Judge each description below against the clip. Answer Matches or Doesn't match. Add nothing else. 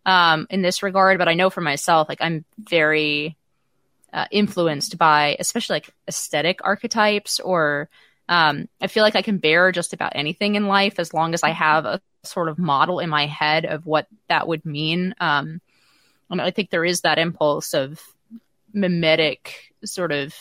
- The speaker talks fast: Doesn't match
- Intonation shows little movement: Doesn't match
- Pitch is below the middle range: Doesn't match